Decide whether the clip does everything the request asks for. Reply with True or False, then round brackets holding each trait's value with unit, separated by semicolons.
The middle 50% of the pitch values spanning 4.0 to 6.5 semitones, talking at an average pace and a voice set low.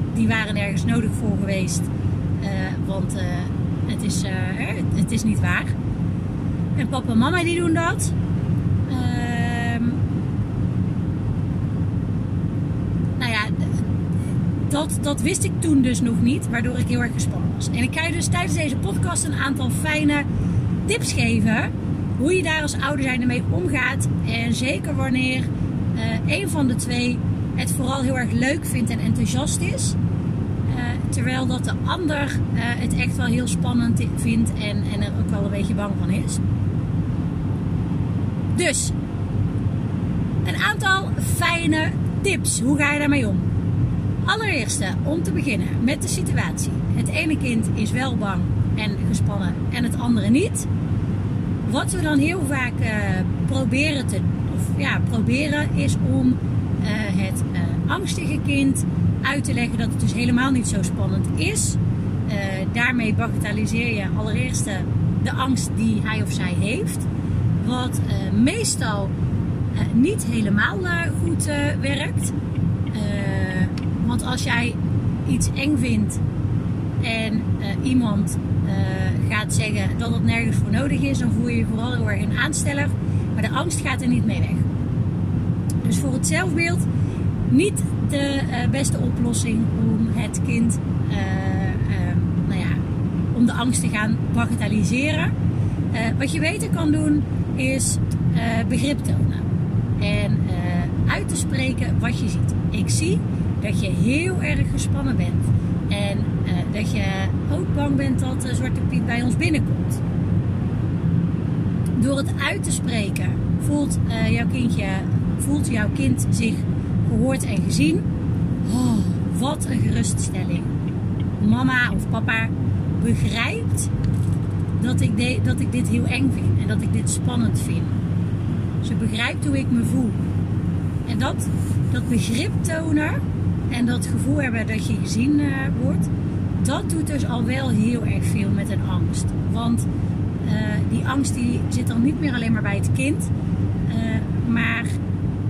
False (3.6 semitones; 150 wpm; 105 Hz)